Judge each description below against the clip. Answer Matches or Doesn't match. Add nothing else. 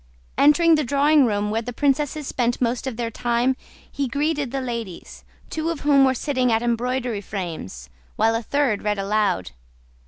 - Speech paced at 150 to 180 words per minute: Matches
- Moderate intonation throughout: Matches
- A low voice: Doesn't match